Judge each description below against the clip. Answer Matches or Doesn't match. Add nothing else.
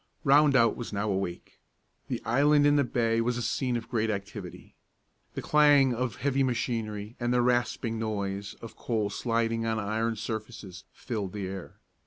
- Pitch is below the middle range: Matches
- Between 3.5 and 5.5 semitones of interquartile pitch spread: Doesn't match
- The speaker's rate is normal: Matches